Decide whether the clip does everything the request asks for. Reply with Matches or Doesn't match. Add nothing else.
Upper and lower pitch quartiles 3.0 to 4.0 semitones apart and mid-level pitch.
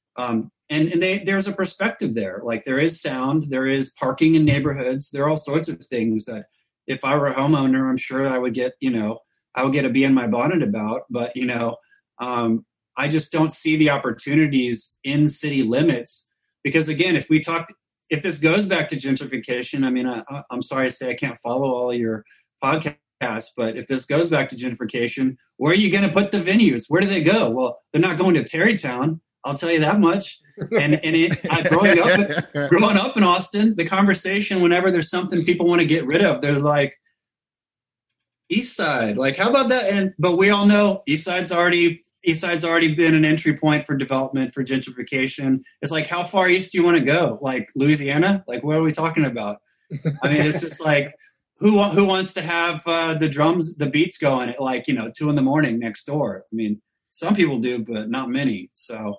Doesn't match